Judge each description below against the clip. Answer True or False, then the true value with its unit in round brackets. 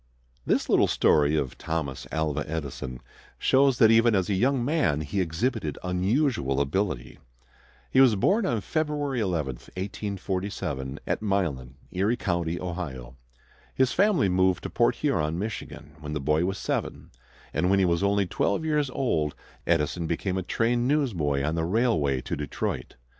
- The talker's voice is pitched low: True (90 Hz)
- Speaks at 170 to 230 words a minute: False (155 wpm)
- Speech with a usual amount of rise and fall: False (7.0 semitones)